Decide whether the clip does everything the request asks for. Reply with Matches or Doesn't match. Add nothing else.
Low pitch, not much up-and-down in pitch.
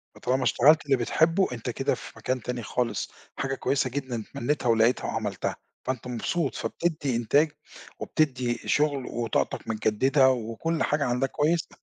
Doesn't match